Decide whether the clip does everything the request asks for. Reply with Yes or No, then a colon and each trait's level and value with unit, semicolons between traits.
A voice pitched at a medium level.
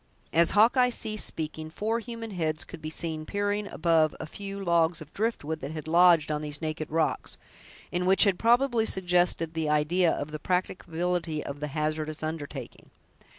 Yes: medium, 165 Hz